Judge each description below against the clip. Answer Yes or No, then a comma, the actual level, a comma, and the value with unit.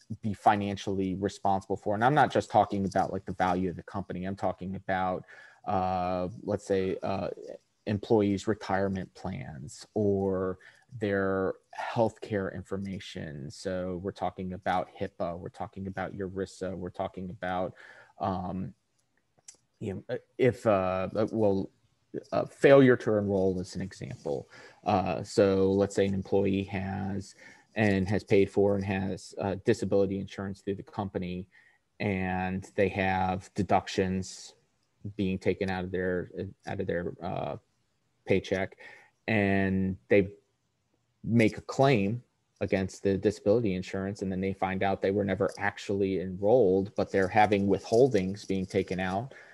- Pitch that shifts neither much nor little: No, narrow, 1.3 semitones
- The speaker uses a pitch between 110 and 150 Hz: No, very low, 95 Hz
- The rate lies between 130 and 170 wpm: Yes, average, 140 wpm